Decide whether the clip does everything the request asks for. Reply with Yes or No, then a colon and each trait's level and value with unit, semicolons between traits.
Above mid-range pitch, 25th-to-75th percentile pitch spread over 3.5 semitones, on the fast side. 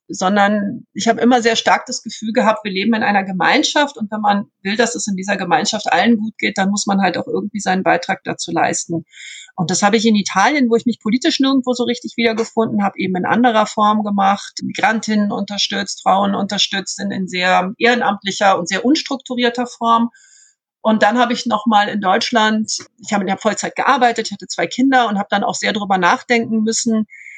No: high, 215 Hz; average, 3.2 semitones; fast, 205 wpm